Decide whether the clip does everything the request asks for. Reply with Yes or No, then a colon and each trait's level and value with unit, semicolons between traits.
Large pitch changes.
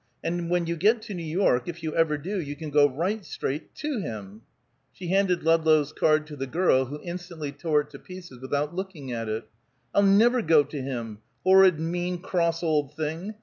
No: average, 3.8 semitones